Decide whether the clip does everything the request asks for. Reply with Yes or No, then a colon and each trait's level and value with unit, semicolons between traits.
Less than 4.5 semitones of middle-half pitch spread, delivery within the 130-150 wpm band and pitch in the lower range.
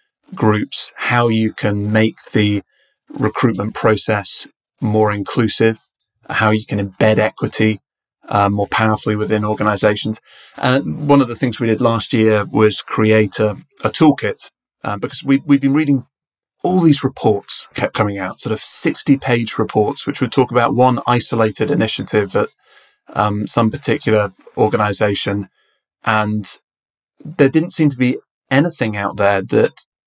Yes: average, 3.8 semitones; average, 145 wpm; low, 110 Hz